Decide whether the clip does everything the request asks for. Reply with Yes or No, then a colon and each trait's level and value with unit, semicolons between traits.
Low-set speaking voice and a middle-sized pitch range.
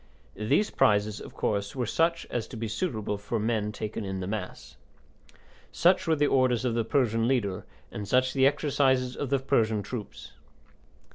Yes: low, 115 Hz; average, 4.1 semitones